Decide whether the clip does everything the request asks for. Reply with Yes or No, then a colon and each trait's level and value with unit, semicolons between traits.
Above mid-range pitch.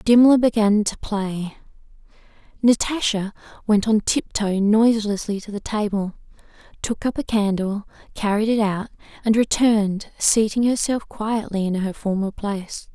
Yes: high, 210 Hz